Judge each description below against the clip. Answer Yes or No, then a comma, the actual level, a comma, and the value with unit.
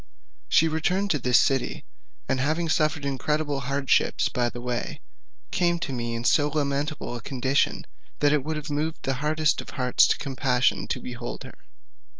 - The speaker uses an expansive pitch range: No, average, 3.3 semitones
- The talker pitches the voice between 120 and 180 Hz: Yes, medium, 140 Hz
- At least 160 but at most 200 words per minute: Yes, average, 165 wpm